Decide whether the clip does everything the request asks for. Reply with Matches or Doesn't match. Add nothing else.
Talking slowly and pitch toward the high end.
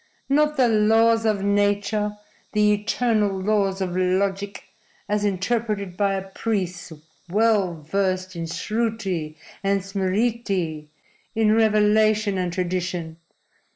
Matches